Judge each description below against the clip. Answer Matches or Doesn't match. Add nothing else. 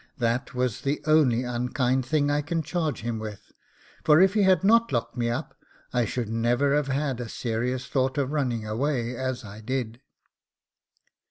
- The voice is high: Doesn't match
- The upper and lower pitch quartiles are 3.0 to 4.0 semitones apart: Matches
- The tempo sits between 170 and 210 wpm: Matches